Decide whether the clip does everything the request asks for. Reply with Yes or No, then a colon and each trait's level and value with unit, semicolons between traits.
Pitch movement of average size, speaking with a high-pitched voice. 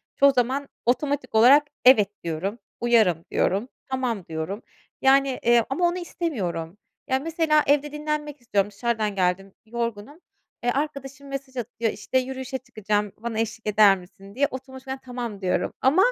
Yes: average, 4.8 semitones; high, 245 Hz